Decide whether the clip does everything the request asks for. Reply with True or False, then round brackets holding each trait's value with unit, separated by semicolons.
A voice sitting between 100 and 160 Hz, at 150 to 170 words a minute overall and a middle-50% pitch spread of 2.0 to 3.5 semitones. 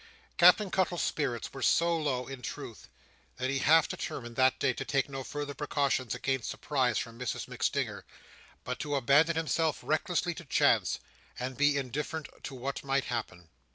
True (140 Hz; 165 wpm; 3.0 semitones)